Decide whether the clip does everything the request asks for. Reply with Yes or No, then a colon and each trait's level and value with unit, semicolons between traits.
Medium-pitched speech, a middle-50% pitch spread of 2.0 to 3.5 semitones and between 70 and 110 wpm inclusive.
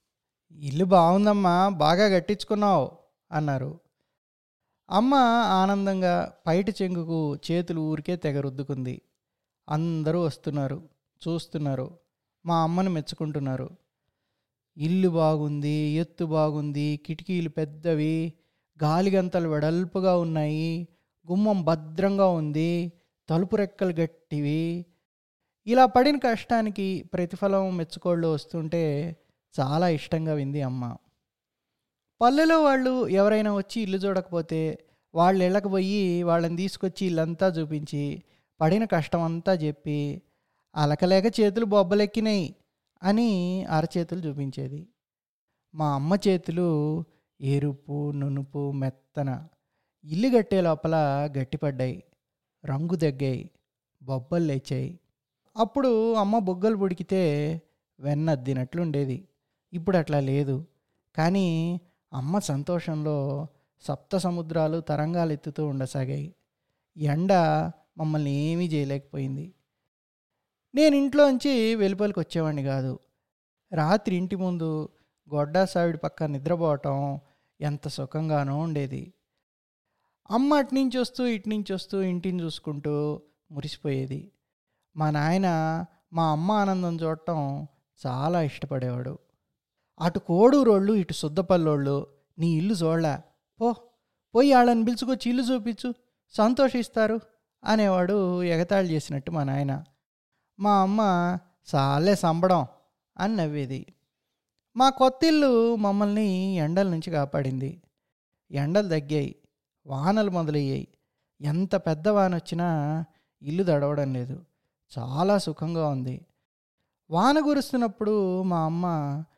No: medium, 165 Hz; average, 4.6 semitones; average, 90 wpm